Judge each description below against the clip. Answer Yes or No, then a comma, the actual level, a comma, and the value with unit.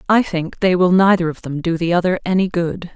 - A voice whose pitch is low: No, medium, 175 Hz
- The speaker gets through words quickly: Yes, fast, 245 wpm